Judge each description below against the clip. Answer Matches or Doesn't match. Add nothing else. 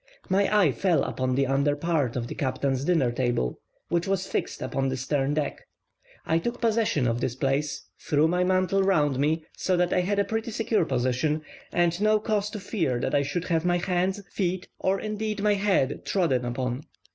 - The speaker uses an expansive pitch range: Matches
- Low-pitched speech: Doesn't match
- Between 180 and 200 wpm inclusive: Matches